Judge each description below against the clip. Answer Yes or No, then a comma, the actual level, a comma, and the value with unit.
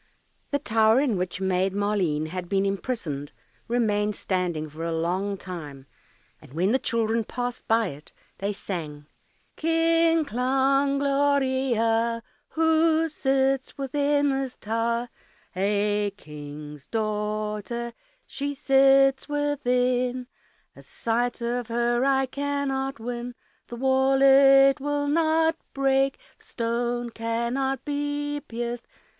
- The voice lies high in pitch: Yes, high, 240 Hz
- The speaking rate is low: Yes, slow, 115 wpm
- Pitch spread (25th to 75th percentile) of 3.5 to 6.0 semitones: Yes, average, 4.7 semitones